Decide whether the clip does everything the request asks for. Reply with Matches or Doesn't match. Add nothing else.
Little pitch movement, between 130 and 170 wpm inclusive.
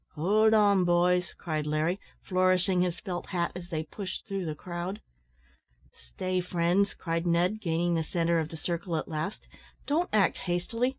Matches